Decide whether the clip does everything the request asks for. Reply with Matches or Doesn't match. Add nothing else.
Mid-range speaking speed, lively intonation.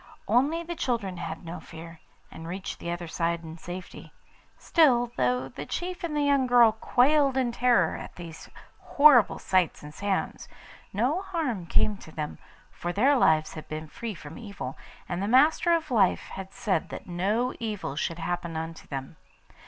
Matches